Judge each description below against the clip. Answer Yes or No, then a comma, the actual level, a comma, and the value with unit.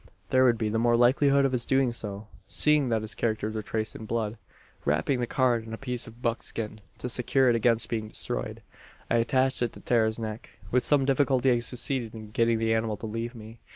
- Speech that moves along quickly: Yes, fast, 220 wpm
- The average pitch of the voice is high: No, low, 115 Hz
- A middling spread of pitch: No, narrow, 2.3 semitones